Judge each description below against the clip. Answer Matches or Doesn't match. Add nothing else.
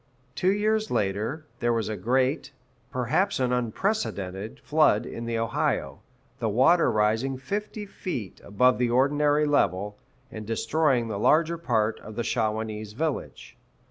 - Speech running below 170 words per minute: Matches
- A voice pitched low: Matches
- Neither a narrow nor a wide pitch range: Doesn't match